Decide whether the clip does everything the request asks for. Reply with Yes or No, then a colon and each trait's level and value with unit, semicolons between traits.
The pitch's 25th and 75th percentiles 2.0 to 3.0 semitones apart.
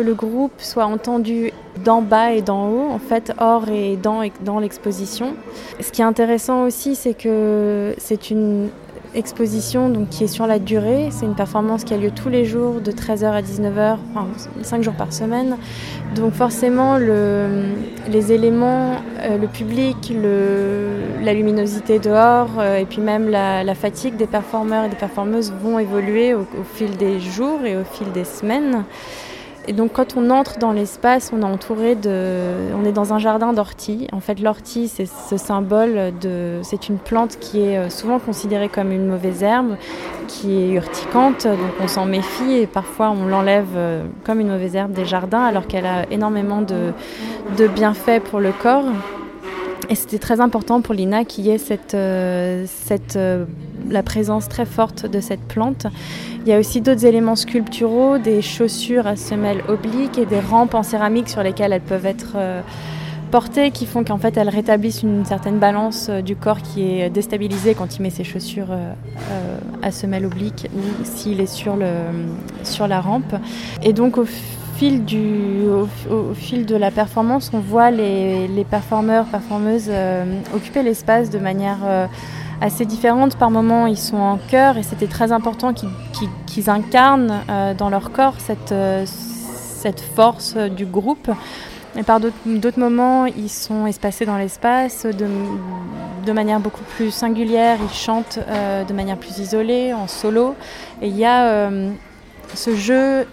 Yes: narrow, 2.6 semitones